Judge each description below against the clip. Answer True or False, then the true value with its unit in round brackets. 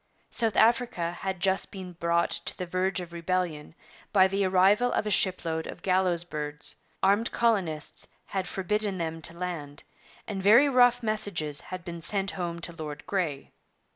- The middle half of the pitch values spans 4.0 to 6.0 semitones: False (3.0 semitones)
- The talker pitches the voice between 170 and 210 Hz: True (185 Hz)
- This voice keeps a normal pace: True (165 wpm)